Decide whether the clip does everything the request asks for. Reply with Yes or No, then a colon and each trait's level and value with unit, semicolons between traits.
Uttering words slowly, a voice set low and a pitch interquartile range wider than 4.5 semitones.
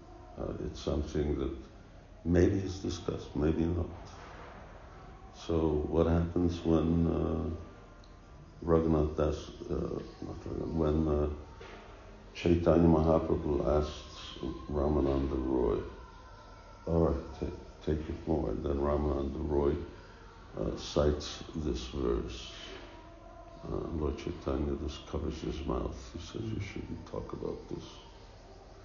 No: slow, 110 wpm; very low, 80 Hz; average, 3.2 semitones